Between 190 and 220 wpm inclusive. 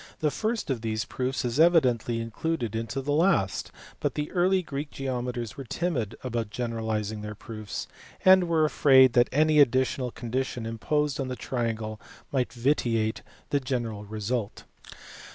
No: average, 150 wpm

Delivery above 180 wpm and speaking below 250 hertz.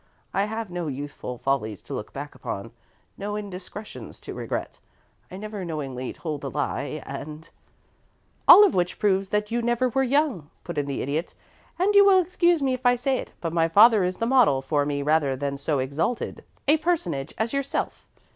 Yes: average, 195 wpm; high, 190 Hz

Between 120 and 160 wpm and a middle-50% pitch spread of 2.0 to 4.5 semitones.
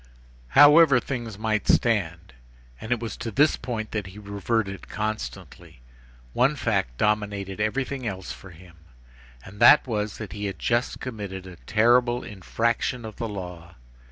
Yes: average, 140 wpm; average, 4.1 semitones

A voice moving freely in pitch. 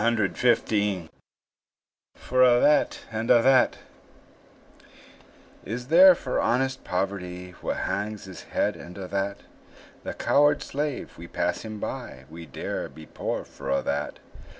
Yes: wide, 5.9 semitones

